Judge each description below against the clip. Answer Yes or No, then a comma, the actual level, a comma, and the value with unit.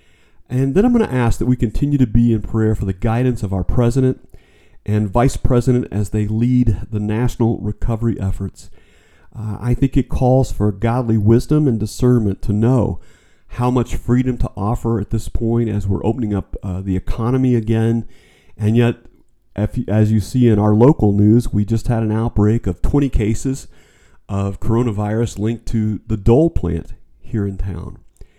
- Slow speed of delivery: No, average, 180 wpm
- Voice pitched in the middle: No, low, 110 Hz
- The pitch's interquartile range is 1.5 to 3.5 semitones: Yes, average, 2.9 semitones